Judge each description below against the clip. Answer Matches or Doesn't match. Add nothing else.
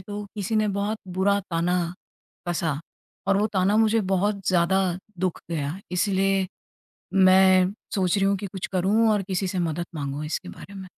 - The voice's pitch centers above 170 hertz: Matches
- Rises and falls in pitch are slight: Matches